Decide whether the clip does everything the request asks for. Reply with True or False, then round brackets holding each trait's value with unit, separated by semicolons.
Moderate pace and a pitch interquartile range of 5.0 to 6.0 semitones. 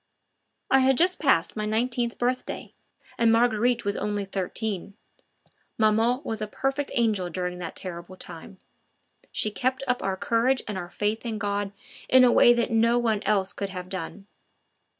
False (165 wpm; 3.8 semitones)